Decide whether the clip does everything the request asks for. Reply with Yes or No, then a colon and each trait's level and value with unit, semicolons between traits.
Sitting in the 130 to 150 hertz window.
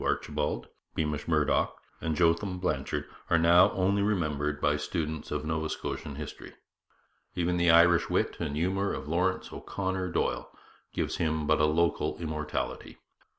No: very low, 80 Hz